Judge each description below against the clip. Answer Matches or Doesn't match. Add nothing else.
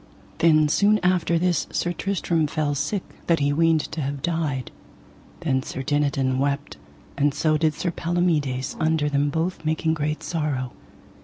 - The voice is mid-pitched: Matches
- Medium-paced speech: Matches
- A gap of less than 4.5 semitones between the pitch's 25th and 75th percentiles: Matches